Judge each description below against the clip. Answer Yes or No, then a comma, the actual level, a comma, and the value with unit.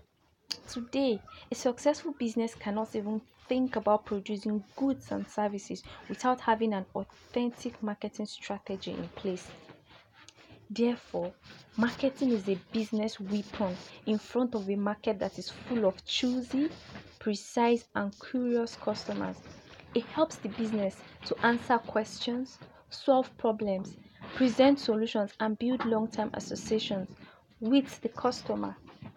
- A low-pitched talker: No, high, 220 Hz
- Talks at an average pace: No, slow, 120 wpm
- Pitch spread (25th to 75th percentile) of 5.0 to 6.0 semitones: No, average, 3.2 semitones